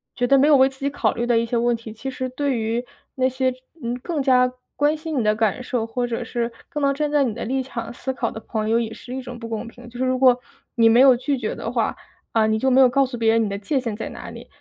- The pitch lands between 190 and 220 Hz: No, high, 245 Hz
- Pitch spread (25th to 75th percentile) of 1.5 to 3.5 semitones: Yes, narrow, 2.5 semitones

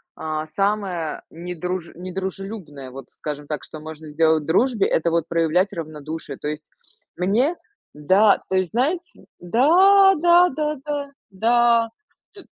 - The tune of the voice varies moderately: No, wide, 7.1 semitones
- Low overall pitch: No, medium, 185 Hz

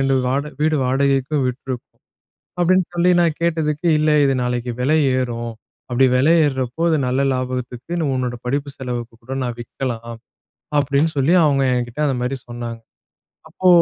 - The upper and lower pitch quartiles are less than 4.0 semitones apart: Yes, average, 3.3 semitones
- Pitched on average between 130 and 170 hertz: Yes, low, 135 Hz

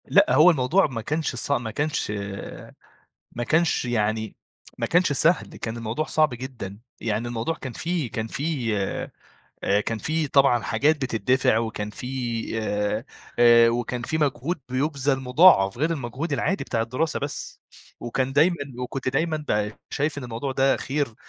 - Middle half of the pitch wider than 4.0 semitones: Yes, average, 4.7 semitones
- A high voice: No, low, 130 Hz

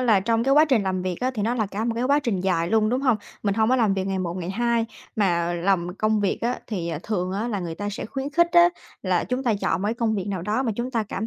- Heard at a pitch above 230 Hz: No, high, 215 Hz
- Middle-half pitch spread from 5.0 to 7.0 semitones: No, average, 4.2 semitones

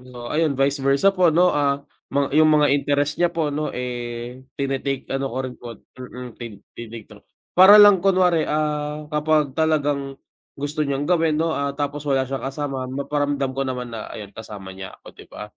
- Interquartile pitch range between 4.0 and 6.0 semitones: No, average, 2.9 semitones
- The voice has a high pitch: No, medium, 140 Hz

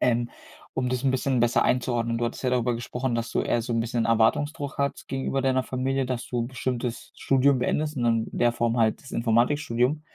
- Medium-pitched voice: No, low, 125 Hz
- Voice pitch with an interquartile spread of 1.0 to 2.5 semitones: Yes, narrow, 2.1 semitones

